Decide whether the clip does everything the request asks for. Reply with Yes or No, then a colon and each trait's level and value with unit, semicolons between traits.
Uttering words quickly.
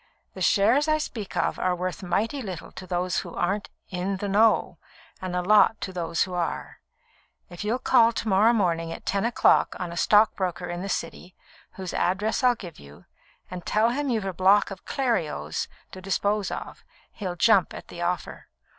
No: average, 190 wpm